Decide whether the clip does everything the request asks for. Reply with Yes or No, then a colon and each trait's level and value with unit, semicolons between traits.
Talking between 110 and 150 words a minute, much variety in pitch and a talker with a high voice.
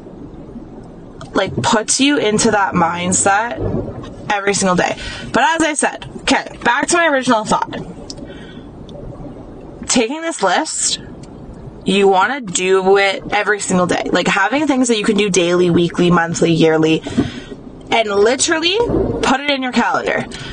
Yes: slow, 135 wpm; wide, 6.3 semitones; high, 205 Hz